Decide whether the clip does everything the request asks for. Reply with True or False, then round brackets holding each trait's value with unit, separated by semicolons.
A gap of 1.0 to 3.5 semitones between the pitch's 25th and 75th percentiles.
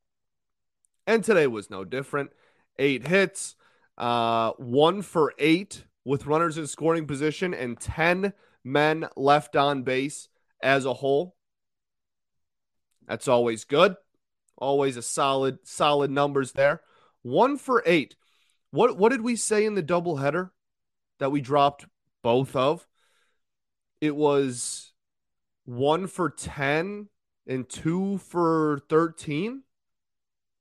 False (5.2 semitones)